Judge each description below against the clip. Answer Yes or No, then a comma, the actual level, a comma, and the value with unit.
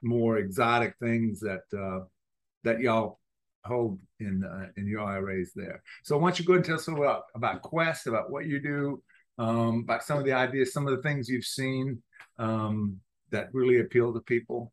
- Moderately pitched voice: No, low, 120 Hz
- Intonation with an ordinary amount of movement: Yes, average, 4.1 semitones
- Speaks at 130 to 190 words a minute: No, fast, 205 wpm